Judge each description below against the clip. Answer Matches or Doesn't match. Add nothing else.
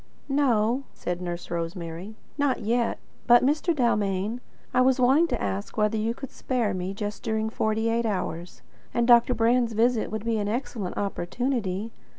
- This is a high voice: Matches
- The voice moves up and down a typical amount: Matches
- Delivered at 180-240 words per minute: Doesn't match